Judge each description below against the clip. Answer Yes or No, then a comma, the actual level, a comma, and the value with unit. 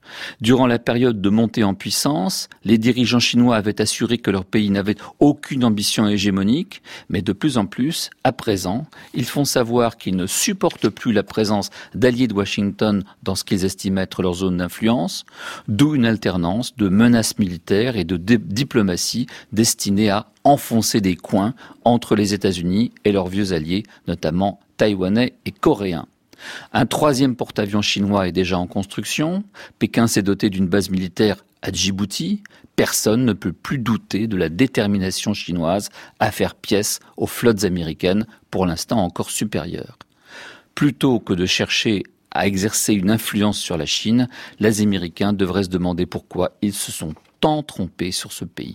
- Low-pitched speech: Yes, low, 105 Hz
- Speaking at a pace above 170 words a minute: No, average, 160 wpm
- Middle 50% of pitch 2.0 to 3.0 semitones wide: No, average, 3.6 semitones